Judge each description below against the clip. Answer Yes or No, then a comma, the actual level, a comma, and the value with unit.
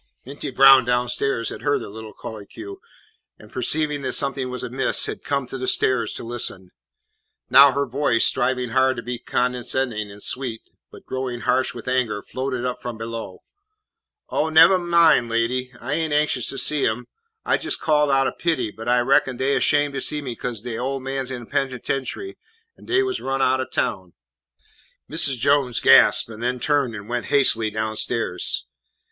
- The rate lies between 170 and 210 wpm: Yes, average, 180 wpm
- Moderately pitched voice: No, low, 130 Hz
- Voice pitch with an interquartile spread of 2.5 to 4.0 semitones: Yes, average, 2.8 semitones